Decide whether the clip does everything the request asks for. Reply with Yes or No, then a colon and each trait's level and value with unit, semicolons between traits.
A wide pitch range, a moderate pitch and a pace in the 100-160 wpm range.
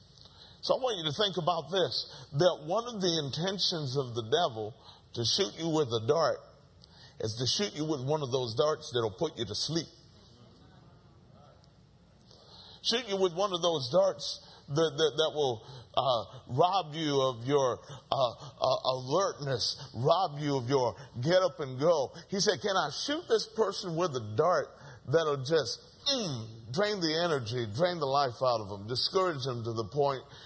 No: wide, 5.9 semitones; medium, 150 Hz; average, 175 wpm